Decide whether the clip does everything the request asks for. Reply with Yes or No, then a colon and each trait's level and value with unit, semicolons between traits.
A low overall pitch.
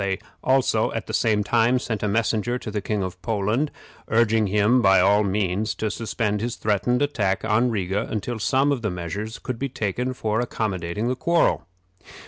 Yes: low, 110 Hz